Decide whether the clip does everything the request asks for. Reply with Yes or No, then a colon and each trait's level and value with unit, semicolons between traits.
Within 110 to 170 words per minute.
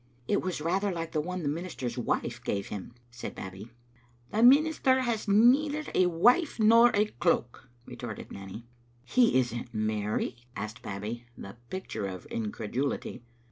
Yes: average, 160 wpm